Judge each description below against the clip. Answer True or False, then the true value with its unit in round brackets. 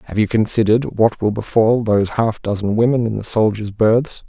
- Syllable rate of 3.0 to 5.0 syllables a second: False (5.4 syllables/s)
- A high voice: False (110 Hz)